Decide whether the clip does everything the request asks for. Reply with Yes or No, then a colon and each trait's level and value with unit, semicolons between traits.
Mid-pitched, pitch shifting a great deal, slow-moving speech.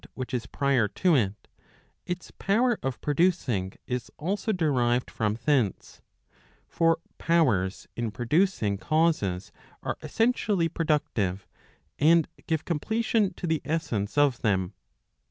Yes: medium, 145 Hz; wide, 7.2 semitones; slow, 120 wpm